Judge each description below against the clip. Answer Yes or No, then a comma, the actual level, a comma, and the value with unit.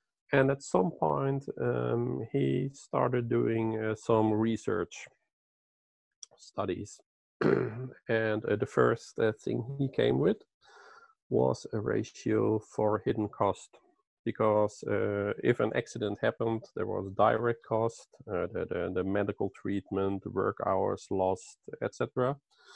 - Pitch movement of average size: Yes, average, 3.8 semitones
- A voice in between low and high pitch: No, low, 110 Hz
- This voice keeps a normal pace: No, slow, 125 wpm